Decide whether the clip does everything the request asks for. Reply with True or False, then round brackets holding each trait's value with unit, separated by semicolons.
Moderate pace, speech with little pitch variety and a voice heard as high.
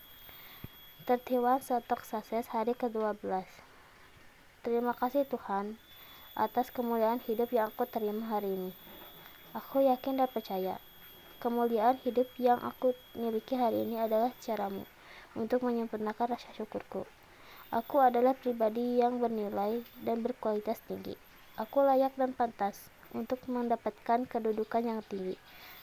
True (115 wpm; 2.1 semitones; 235 Hz)